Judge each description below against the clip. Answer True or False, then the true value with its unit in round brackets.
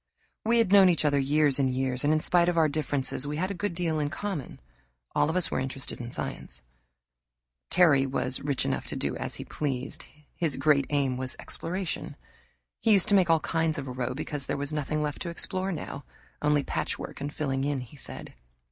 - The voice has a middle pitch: True (150 Hz)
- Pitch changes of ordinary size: True (3.9 semitones)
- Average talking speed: False (210 wpm)